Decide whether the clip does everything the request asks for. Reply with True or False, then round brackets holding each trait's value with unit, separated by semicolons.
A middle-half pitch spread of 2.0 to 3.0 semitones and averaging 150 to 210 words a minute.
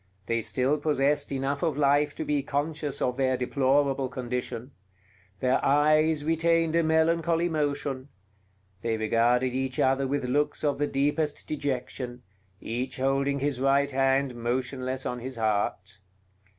False (2.5 semitones; 135 wpm)